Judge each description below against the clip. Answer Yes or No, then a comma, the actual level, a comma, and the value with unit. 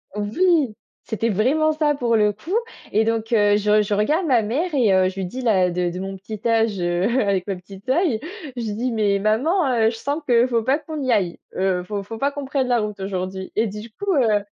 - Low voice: No, high, 220 Hz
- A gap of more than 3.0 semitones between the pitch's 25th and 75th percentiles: Yes, average, 4.6 semitones